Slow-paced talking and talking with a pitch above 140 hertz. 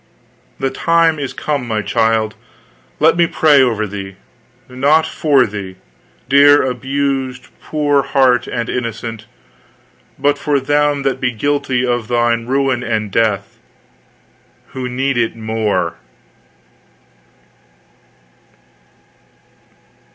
No: slow, 105 wpm; low, 125 Hz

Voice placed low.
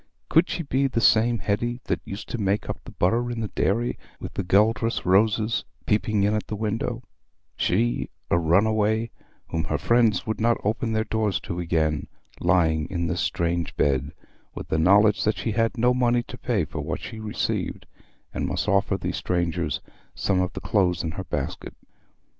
Yes: low, 105 Hz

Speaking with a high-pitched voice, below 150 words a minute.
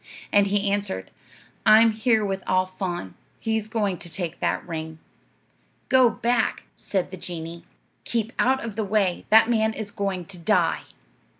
No: high, 200 Hz; average, 160 wpm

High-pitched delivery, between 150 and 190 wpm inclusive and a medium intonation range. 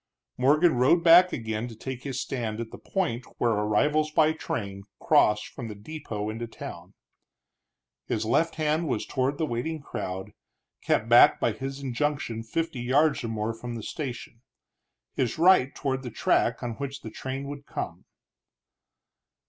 No: low, 130 Hz; average, 155 wpm; average, 4.8 semitones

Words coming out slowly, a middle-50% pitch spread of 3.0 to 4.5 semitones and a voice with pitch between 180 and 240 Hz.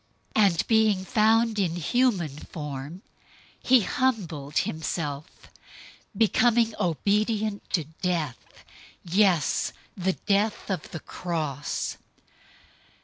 No: slow, 90 wpm; average, 5.3 semitones; high, 190 Hz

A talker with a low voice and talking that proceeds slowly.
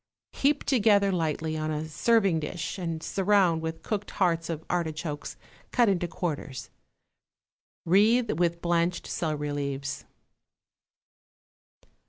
No: medium, 170 Hz; slow, 110 wpm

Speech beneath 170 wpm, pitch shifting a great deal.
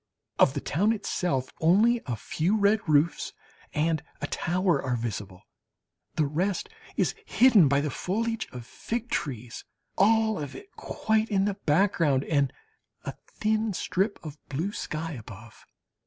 Yes: average, 145 wpm; wide, 6.9 semitones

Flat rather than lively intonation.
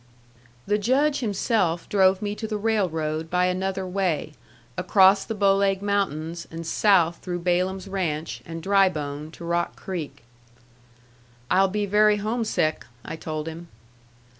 No: average, 3.6 semitones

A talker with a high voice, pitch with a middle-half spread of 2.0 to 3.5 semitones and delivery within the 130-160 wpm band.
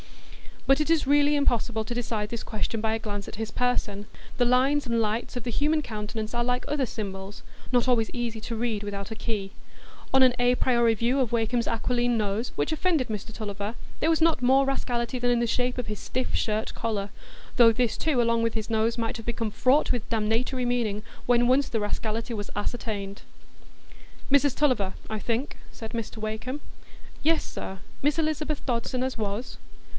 No: high, 235 Hz; average, 2.7 semitones; average, 190 wpm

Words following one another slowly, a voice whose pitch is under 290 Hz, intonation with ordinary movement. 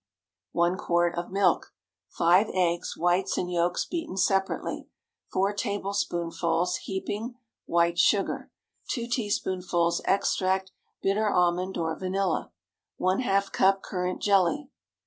No: slow, 110 wpm; medium, 185 Hz; narrow, 2.3 semitones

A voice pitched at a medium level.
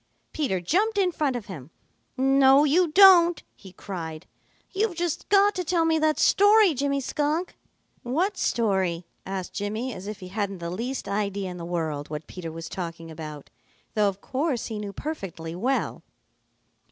No: high, 225 Hz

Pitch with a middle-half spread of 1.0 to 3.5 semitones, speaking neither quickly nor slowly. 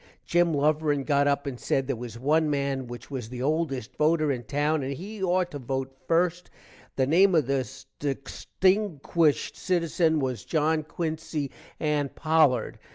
Yes: average, 3.2 semitones; average, 160 wpm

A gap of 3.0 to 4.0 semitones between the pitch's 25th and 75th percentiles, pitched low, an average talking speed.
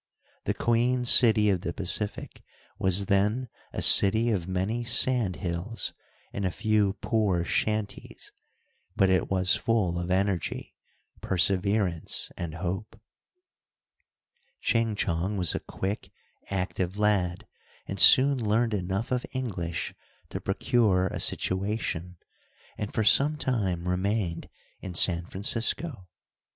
No: average, 3.6 semitones; low, 100 Hz; slow, 120 wpm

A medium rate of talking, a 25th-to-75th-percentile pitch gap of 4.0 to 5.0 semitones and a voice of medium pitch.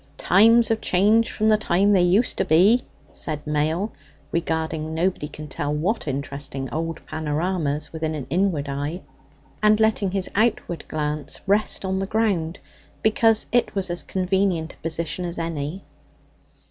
Yes: average, 150 wpm; average, 4.6 semitones; medium, 175 Hz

